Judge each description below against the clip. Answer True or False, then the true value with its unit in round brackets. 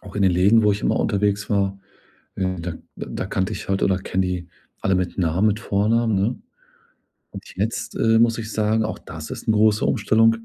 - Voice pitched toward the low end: True (100 Hz)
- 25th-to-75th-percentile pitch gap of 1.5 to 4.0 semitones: True (2.7 semitones)